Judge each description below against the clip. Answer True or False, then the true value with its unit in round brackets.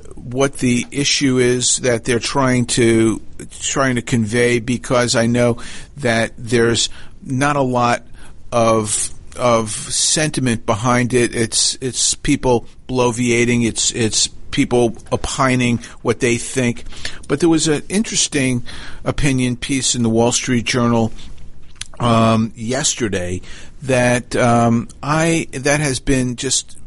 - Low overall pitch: True (120 Hz)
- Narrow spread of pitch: True (2.3 semitones)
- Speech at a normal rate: False (125 wpm)